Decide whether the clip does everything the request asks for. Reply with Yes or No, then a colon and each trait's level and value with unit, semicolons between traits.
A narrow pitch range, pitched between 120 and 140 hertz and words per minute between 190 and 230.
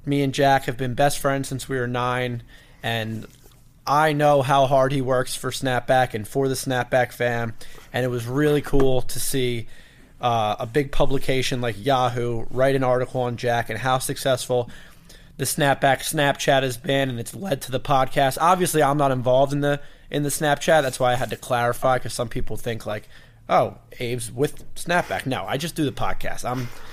Yes: narrow, 2.3 semitones; low, 130 Hz; average, 195 wpm